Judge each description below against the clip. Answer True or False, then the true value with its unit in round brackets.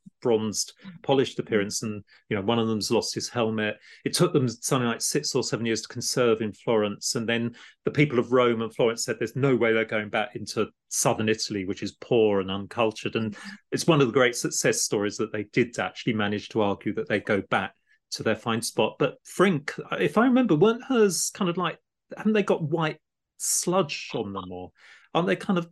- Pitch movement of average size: False (6.4 semitones)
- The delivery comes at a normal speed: False (215 wpm)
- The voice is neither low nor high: False (115 Hz)